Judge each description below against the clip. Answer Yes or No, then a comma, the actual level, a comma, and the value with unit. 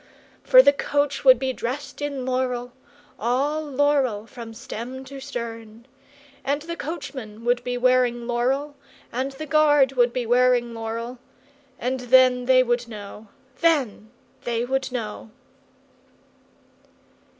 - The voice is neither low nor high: No, very high, 255 Hz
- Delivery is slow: Yes, slow, 130 wpm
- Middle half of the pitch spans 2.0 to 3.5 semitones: Yes, narrow, 2.5 semitones